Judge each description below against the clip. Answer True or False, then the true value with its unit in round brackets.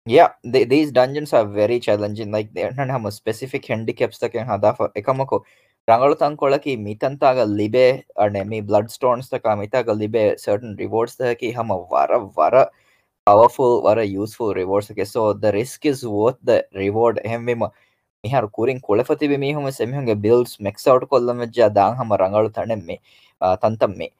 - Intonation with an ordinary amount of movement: True (4.2 semitones)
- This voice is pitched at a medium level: False (115 Hz)